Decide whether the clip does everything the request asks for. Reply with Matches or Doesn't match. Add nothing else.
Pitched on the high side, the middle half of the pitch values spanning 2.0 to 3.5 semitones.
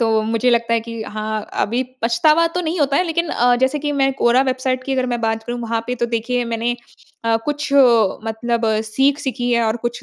Matches